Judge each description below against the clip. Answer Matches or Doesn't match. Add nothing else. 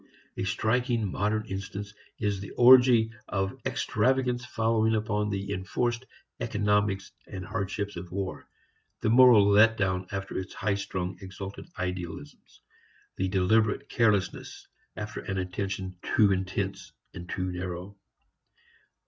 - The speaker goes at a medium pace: Doesn't match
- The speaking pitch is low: Matches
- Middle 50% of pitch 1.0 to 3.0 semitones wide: Matches